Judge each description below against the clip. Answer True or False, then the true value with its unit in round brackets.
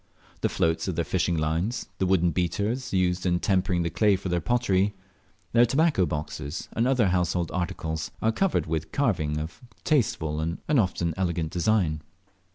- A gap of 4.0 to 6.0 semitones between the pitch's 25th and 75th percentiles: True (4.5 semitones)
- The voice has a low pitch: True (90 Hz)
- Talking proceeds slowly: False (165 wpm)